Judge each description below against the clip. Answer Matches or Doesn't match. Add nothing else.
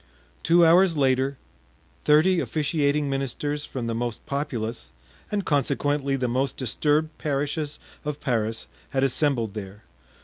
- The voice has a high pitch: Doesn't match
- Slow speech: Matches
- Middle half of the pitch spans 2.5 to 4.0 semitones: Matches